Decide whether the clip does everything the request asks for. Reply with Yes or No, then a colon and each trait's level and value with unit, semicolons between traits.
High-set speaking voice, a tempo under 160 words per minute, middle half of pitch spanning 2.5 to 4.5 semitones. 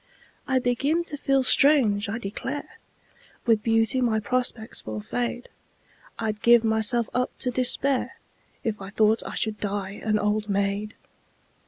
Yes: high, 225 Hz; average, 145 wpm; average, 3.2 semitones